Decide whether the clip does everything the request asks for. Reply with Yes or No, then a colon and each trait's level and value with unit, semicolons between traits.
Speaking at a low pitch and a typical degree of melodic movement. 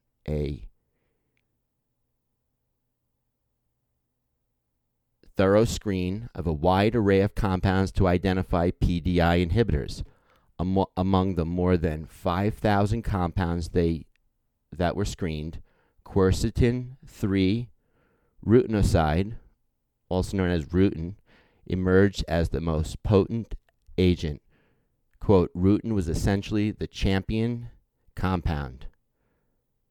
Yes: very low, 95 Hz; average, 3.4 semitones